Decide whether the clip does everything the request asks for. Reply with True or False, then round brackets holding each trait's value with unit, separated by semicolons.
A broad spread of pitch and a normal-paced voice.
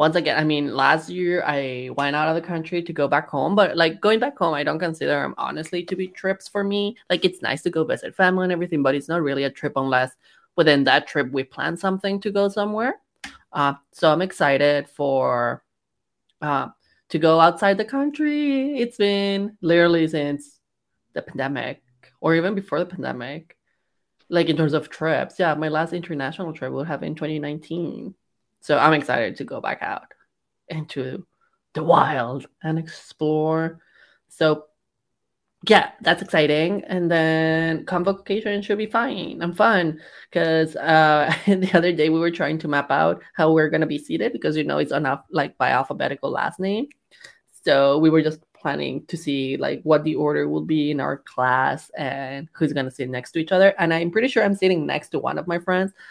False (4.1 semitones; 190 wpm)